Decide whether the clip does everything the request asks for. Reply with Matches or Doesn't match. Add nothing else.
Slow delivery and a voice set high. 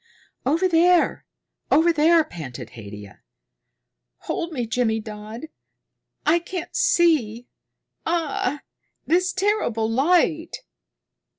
Matches